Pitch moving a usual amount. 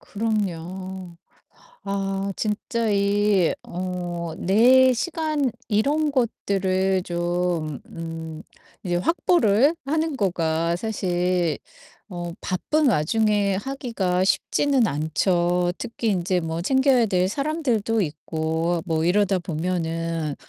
Yes: average, 4.7 semitones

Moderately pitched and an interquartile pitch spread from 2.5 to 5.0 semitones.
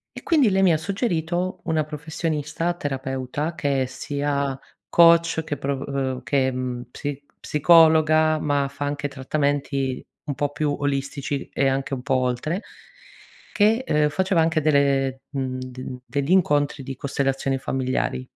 Yes: medium, 145 Hz; average, 2.8 semitones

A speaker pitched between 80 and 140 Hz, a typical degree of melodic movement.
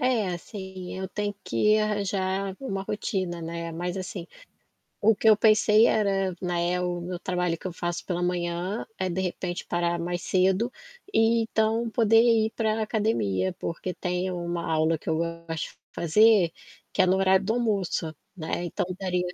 No: medium, 185 Hz; average, 3.5 semitones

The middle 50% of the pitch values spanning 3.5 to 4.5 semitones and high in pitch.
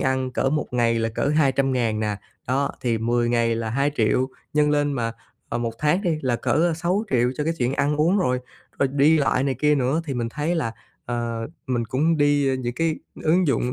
No: average, 3.9 semitones; low, 135 Hz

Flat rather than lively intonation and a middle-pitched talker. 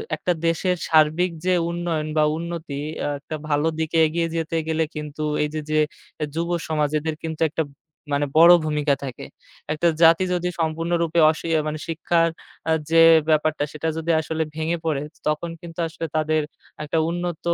Yes: narrow, 1.6 semitones; medium, 160 Hz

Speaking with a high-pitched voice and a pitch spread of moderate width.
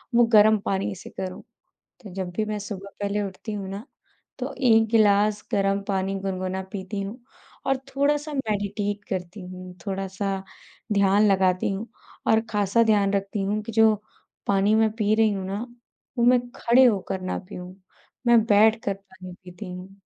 No: high, 200 Hz; narrow, 2.2 semitones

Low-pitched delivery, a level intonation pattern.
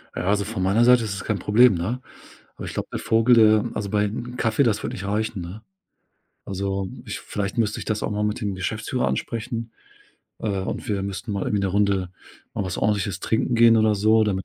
Yes: low, 105 Hz; narrow, 2.2 semitones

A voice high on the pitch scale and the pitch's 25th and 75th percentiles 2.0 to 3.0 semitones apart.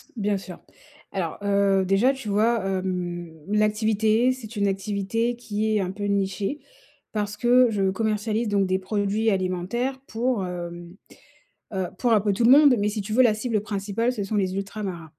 Yes: high, 205 Hz; narrow, 2.6 semitones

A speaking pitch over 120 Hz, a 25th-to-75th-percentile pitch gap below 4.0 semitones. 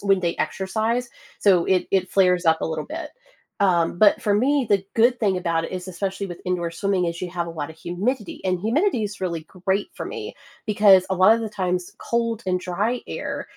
Yes: high, 190 Hz; average, 3.4 semitones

